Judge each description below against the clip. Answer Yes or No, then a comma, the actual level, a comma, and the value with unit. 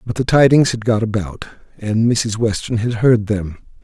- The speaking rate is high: No, average, 190 wpm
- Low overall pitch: Yes, low, 115 Hz